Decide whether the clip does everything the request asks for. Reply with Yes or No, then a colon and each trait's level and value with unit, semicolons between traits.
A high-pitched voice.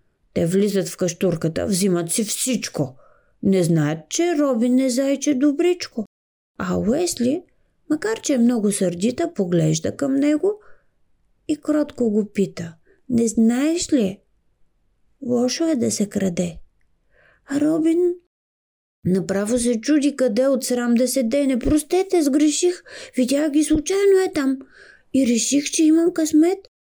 Yes: very high, 265 Hz